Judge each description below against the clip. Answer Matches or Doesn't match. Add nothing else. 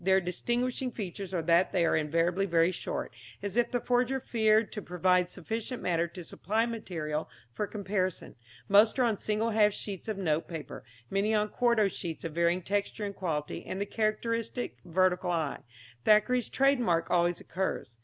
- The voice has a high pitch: Matches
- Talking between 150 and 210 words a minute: Matches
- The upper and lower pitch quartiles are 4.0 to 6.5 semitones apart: Matches